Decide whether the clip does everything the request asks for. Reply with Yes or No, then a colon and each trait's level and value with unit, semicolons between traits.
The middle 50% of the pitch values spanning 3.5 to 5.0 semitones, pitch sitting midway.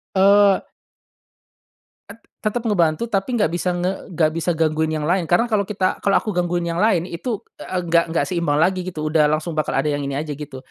Yes: average, 3.8 semitones; medium, 175 Hz